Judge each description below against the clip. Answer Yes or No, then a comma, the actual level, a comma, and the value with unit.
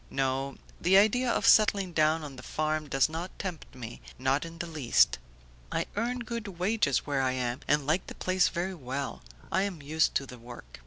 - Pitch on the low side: No, medium, 155 Hz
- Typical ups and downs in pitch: No, wide, 5.7 semitones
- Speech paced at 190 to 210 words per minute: Yes, average, 195 wpm